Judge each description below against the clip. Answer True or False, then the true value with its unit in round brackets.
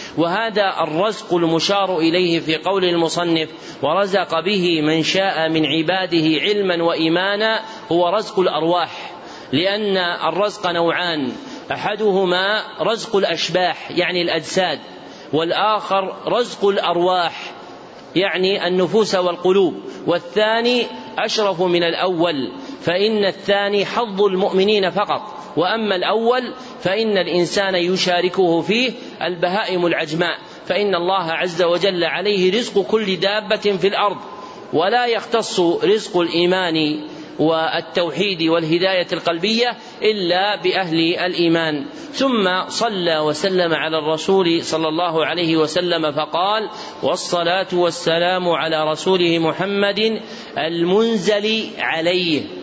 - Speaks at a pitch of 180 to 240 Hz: True (185 Hz)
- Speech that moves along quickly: False (100 wpm)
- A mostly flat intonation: False (3.3 semitones)